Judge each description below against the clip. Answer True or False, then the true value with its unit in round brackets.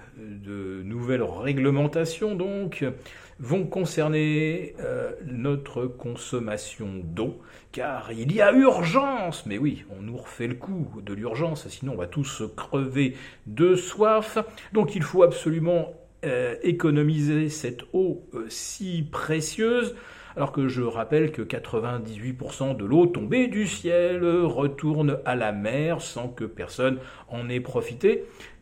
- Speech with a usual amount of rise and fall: False (6.3 semitones)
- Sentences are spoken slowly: True (130 wpm)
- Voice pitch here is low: False (145 Hz)